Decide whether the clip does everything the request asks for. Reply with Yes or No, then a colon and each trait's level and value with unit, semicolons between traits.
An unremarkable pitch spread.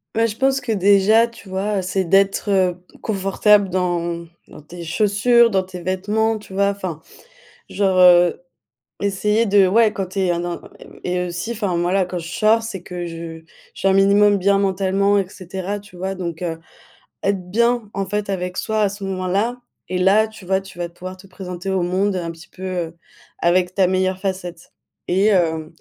No: narrow, 2.2 semitones